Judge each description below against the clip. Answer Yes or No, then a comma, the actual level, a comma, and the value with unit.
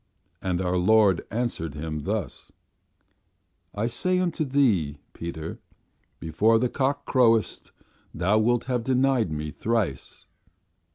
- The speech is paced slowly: Yes, slow, 115 wpm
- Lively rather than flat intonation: Yes, wide, 6.7 semitones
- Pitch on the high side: No, low, 110 Hz